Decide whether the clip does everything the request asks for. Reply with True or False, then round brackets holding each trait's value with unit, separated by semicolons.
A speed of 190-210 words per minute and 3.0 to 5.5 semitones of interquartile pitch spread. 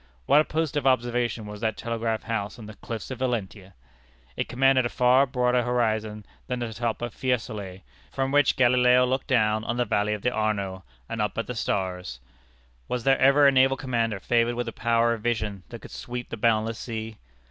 False (200 wpm; 2.5 semitones)